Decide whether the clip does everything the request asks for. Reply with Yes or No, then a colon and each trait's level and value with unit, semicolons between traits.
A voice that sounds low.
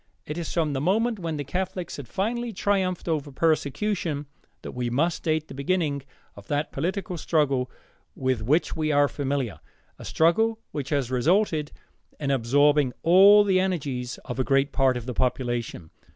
No: medium, 150 Hz